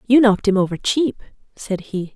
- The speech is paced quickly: No, average, 195 wpm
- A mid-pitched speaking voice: No, high, 210 Hz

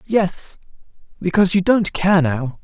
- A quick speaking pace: No, slow, 115 wpm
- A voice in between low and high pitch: Yes, medium, 180 Hz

